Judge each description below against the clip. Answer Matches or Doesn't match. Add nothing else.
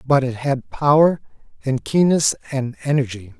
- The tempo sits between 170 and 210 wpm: Doesn't match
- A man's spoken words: Matches